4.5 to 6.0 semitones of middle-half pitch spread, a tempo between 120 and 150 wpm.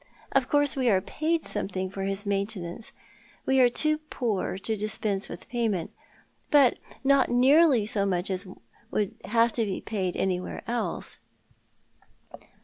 Yes: average, 4.9 semitones; average, 145 wpm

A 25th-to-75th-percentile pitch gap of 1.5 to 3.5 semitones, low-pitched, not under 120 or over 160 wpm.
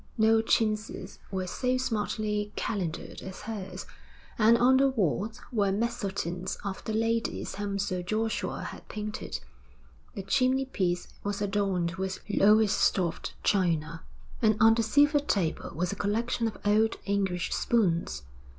No: average, 2.9 semitones; high, 210 Hz; slow, 135 wpm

